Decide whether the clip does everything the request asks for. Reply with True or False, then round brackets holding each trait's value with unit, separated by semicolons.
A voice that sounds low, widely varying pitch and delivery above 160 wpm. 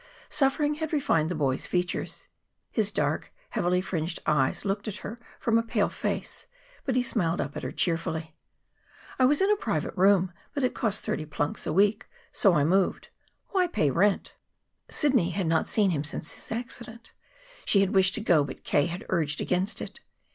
False (190 Hz; 6.0 semitones; 185 wpm)